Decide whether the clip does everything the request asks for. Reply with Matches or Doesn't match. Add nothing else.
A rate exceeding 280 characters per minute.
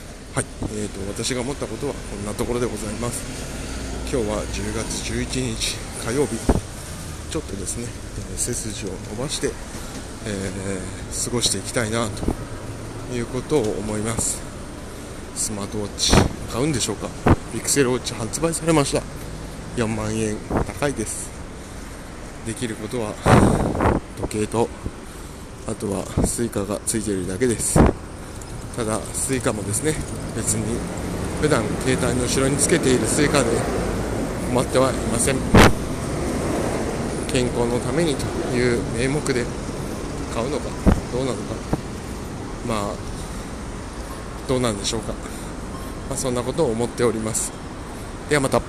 Doesn't match